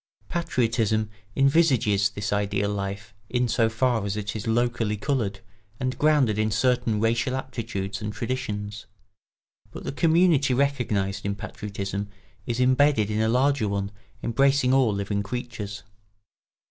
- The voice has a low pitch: Yes, low, 110 Hz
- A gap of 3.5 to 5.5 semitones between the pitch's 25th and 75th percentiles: Yes, average, 3.9 semitones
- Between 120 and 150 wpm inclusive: Yes, slow, 135 wpm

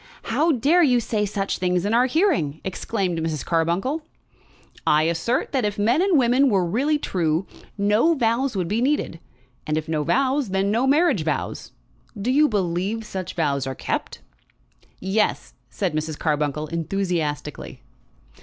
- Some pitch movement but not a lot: No, wide, 7.4 semitones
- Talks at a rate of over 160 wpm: No, average, 155 wpm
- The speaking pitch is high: Yes, high, 200 Hz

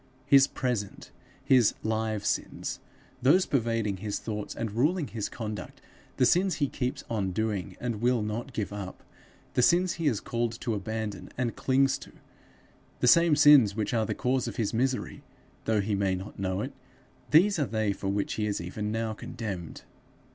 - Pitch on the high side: No, low, 115 Hz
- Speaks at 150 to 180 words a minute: Yes, average, 175 wpm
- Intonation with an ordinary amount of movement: Yes, average, 3.8 semitones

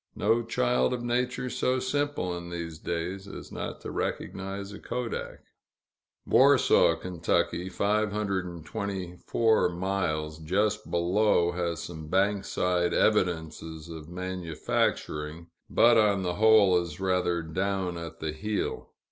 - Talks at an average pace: No, slow, 115 wpm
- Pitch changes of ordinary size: Yes, average, 3.8 semitones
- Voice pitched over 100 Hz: No, very low, 95 Hz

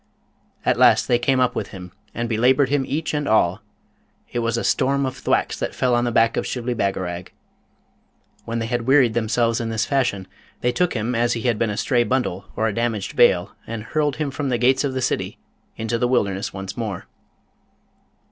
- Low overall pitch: Yes, low, 120 Hz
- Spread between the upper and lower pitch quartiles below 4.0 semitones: Yes, average, 2.7 semitones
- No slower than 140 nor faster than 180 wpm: No, fast, 205 wpm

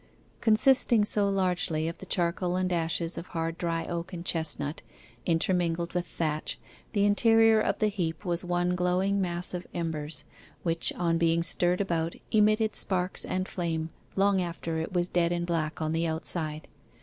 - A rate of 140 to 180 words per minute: Yes, average, 165 wpm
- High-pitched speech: No, medium, 175 Hz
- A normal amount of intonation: No, narrow, 2.2 semitones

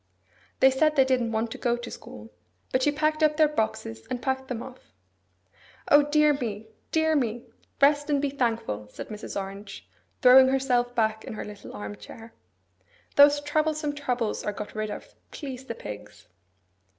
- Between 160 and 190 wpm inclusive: Yes, average, 175 wpm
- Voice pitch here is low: No, very high, 250 Hz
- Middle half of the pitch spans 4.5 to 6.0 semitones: Yes, average, 4.8 semitones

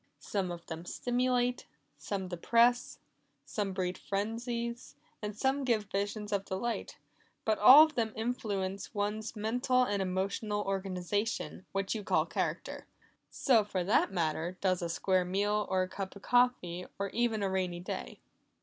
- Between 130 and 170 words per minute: Yes, average, 150 wpm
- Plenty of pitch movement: No, average, 3.8 semitones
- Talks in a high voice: Yes, high, 205 Hz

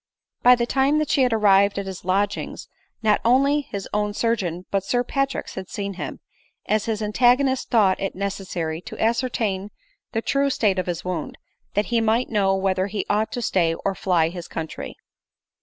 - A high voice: Yes, high, 205 Hz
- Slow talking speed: No, average, 185 wpm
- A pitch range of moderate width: Yes, average, 3.9 semitones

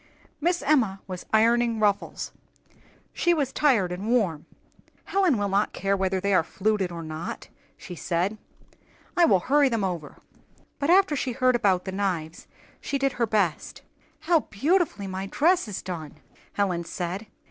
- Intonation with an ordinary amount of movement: No, wide, 6.4 semitones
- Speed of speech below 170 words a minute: Yes, average, 160 wpm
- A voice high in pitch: Yes, high, 205 Hz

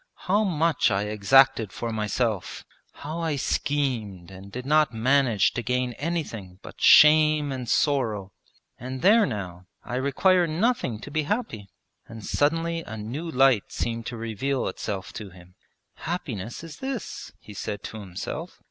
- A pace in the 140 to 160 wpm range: Yes, average, 150 wpm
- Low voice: Yes, low, 125 Hz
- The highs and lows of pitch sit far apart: Yes, wide, 6.5 semitones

